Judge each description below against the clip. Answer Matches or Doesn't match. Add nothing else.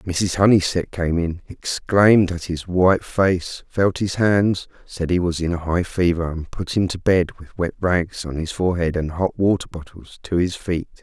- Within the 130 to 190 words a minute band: Doesn't match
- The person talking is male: Matches